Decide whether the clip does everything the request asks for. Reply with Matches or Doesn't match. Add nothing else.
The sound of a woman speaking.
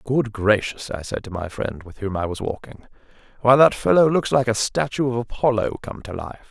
Doesn't match